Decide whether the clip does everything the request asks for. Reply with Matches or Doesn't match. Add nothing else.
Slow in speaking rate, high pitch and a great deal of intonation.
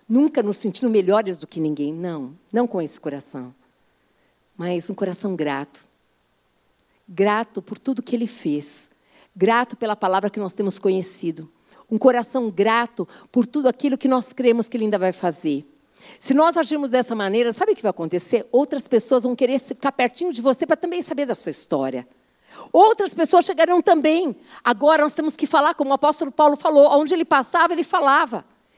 Doesn't match